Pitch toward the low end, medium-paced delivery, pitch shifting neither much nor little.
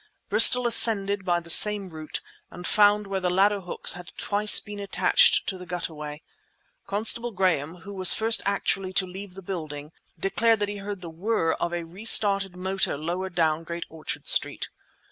No: high, 190 Hz; average, 180 wpm; average, 3.0 semitones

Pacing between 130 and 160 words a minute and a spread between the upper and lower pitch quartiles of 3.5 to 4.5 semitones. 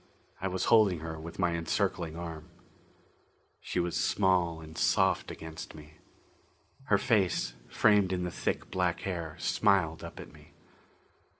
No: average, 140 wpm; average, 2.8 semitones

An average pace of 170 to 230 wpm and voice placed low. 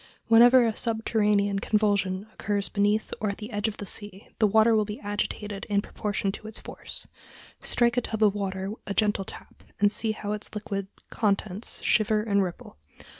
No: average, 180 wpm; high, 210 Hz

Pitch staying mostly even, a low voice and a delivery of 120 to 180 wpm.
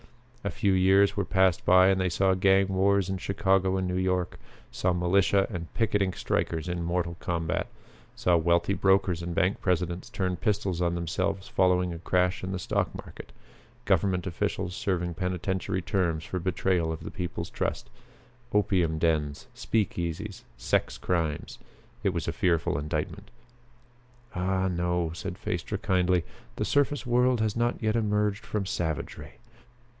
Yes: narrow, 2.0 semitones; very low, 90 Hz; average, 150 wpm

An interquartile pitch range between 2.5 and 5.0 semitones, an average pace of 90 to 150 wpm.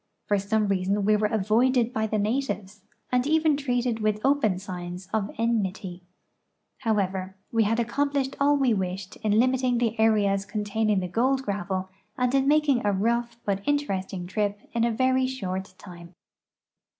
No: average, 4.2 semitones; average, 160 wpm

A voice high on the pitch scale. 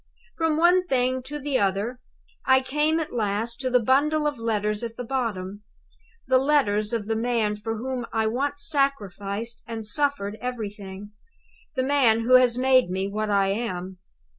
Yes: high, 235 Hz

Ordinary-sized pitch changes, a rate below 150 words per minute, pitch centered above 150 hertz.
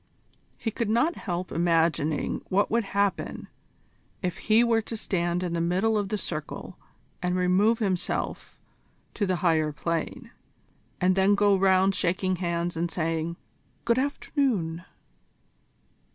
Yes: average, 3.8 semitones; slow, 135 wpm; medium, 185 Hz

